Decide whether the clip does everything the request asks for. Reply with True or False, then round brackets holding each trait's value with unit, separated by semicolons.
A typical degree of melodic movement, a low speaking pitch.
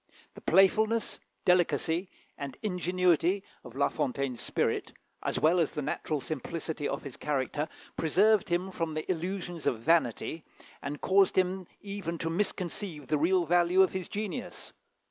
False (3.6 semitones; 170 Hz)